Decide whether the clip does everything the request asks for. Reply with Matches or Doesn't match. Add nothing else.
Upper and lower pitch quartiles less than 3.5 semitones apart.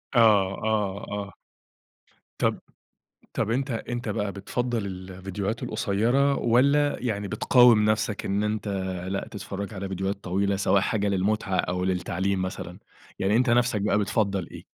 Matches